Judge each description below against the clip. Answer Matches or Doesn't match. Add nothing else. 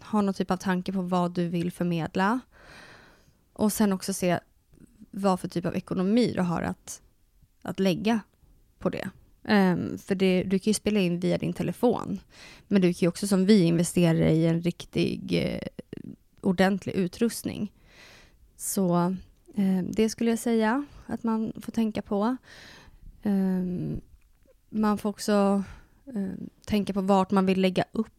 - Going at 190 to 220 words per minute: Doesn't match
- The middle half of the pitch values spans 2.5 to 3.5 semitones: Matches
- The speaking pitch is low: Doesn't match